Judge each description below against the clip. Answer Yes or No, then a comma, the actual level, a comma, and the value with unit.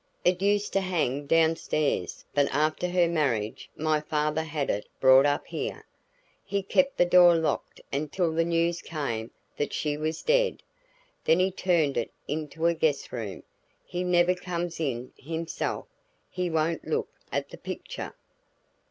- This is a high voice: No, medium, 160 Hz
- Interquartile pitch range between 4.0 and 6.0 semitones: No, average, 3.3 semitones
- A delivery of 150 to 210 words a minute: Yes, average, 155 wpm